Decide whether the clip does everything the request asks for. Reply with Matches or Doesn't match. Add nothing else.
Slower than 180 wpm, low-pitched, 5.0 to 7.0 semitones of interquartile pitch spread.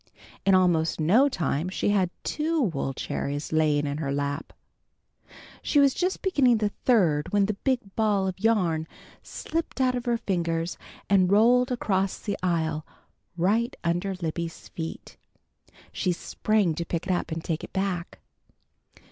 Doesn't match